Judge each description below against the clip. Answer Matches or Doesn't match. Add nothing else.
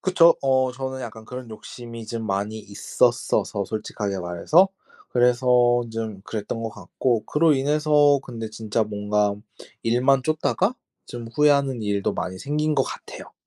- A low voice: Matches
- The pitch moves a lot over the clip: Doesn't match